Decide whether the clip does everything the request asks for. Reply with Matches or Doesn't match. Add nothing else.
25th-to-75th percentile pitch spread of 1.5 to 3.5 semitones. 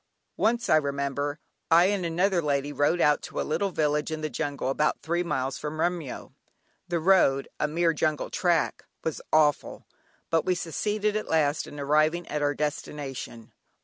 Matches